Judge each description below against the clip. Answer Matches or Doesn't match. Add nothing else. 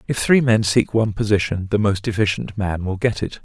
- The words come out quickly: Matches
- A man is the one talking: Matches